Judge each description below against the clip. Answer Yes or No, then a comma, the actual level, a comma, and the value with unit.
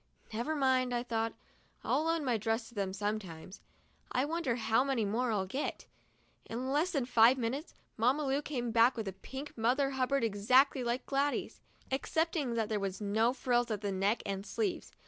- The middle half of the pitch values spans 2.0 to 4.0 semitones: Yes, average, 3.7 semitones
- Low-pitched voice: No, high, 240 Hz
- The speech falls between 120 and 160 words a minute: No, average, 185 wpm